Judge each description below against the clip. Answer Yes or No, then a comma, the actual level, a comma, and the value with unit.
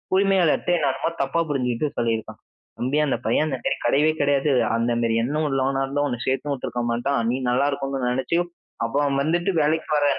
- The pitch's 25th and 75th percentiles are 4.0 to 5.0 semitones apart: No, average, 3.4 semitones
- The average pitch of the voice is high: No, medium, 140 Hz